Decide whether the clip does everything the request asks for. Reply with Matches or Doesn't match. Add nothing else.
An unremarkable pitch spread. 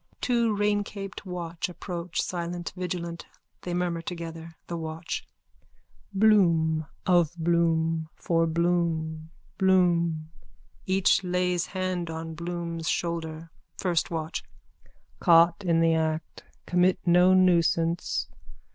Doesn't match